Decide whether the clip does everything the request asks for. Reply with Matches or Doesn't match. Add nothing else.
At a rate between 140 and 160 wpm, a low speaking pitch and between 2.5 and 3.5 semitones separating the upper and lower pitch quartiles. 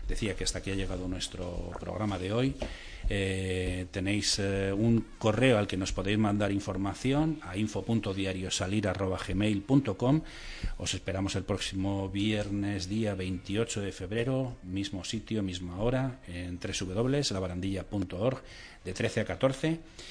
Doesn't match